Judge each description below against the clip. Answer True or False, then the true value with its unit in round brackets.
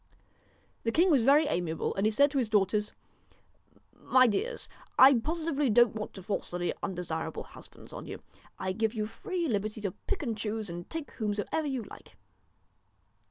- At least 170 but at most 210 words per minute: True (175 wpm)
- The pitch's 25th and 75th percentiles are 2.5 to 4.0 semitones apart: False (5.6 semitones)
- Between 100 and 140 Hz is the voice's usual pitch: False (220 Hz)